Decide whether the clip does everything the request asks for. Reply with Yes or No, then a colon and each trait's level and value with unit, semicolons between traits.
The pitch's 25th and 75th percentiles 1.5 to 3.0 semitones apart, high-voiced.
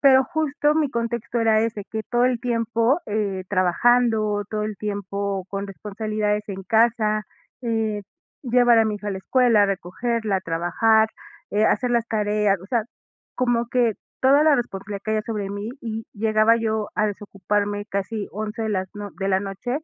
Yes: narrow, 2.5 semitones; high, 215 Hz